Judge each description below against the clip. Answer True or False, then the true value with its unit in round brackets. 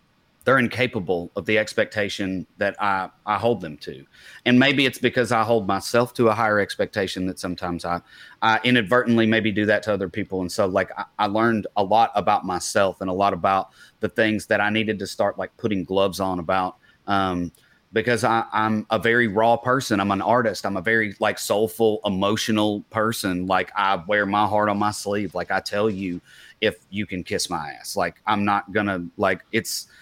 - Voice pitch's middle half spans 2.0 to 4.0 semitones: True (2.6 semitones)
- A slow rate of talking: False (200 wpm)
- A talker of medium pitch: False (105 Hz)